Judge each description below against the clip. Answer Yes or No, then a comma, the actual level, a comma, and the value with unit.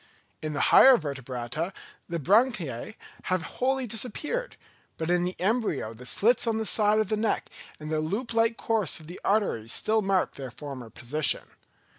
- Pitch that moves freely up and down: Yes, wide, 7.0 semitones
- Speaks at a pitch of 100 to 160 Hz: No, medium, 185 Hz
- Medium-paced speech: Yes, average, 165 wpm